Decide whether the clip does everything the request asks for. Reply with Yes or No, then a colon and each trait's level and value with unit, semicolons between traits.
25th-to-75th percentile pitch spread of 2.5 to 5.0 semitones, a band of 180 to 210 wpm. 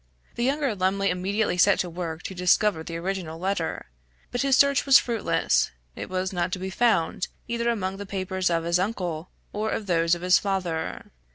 Yes: average, 3.3 semitones; average, 185 wpm